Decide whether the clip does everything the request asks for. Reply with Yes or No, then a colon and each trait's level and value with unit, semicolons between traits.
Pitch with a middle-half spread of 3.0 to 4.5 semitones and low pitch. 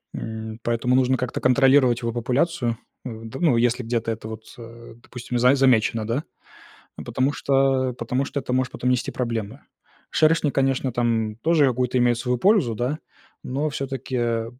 No: narrow, 2.4 semitones; low, 125 Hz